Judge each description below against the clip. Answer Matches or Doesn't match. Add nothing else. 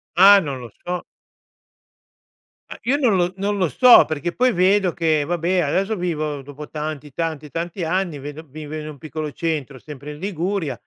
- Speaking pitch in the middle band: Matches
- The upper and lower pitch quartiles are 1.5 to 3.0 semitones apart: Doesn't match